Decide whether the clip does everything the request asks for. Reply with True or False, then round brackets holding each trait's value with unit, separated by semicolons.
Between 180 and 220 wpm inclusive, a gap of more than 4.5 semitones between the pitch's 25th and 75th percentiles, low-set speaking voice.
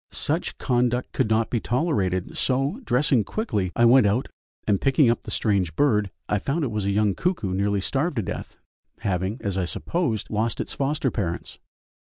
True (185 wpm; 5.2 semitones; 110 Hz)